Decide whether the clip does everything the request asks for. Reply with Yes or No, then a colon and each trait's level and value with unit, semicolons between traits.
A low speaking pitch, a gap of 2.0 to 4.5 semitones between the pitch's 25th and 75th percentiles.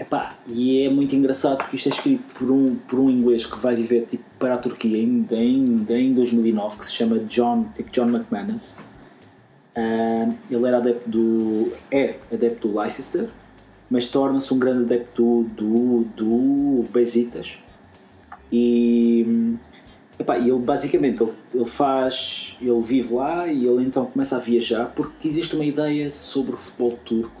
Yes: low, 120 Hz; narrow, 2.5 semitones